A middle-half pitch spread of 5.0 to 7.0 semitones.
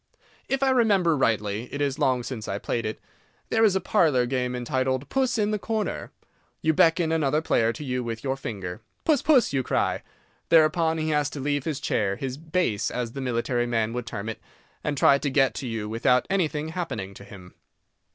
Yes: wide, 5.6 semitones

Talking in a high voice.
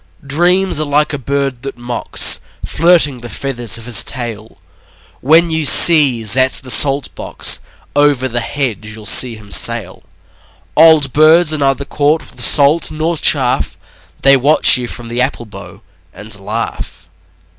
No: low, 135 Hz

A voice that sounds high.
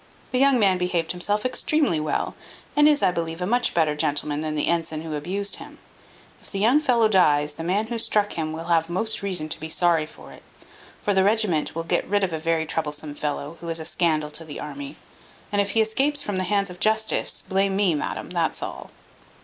No: medium, 175 Hz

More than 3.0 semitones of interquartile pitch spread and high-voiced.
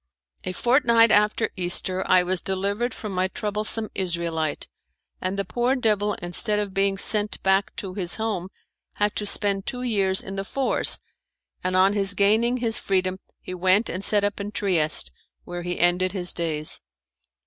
No: narrow, 2.4 semitones; high, 195 Hz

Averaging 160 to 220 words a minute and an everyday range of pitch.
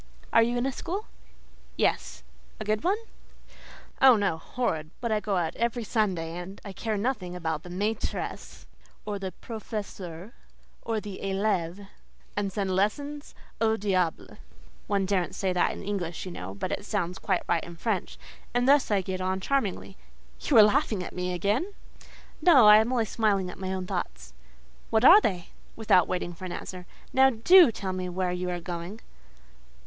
Yes: average, 170 wpm; average, 3.7 semitones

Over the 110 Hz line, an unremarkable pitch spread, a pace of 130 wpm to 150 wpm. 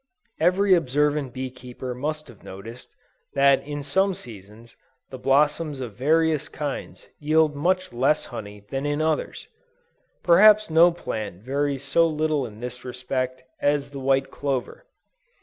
Yes: medium, 140 Hz; average, 3.6 semitones; average, 140 wpm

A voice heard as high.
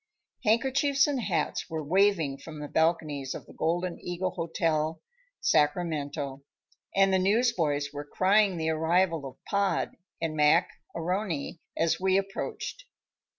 No: medium, 170 Hz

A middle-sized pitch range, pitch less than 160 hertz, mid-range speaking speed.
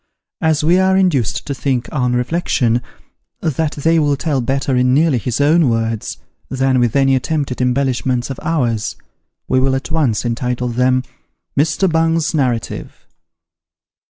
Yes: average, 4.0 semitones; low, 135 Hz; average, 145 wpm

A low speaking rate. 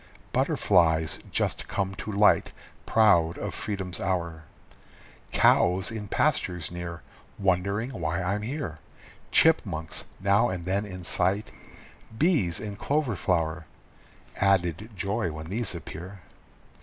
Yes: slow, 115 wpm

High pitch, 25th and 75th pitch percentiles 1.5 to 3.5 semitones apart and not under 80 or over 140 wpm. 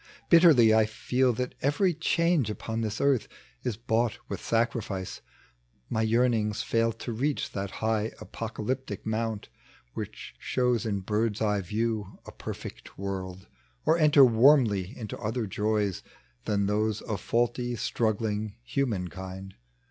No: low, 110 Hz; average, 2.9 semitones; slow, 135 wpm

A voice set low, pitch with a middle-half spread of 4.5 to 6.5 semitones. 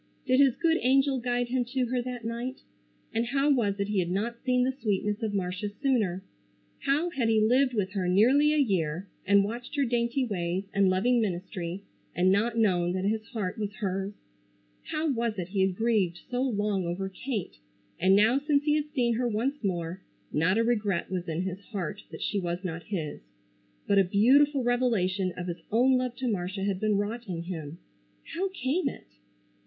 No: high, 215 Hz; average, 5.1 semitones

